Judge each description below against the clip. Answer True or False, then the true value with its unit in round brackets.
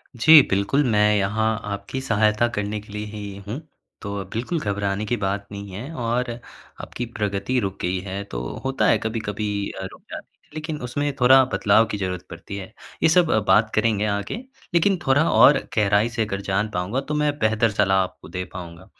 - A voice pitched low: True (105 Hz)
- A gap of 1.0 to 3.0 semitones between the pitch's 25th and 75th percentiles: False (3.5 semitones)